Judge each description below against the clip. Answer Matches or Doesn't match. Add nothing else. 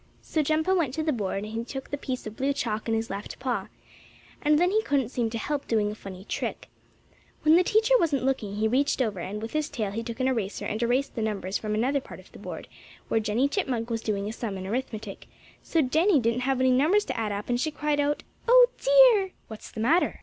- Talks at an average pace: Doesn't match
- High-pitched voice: Matches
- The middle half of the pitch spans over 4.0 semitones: Matches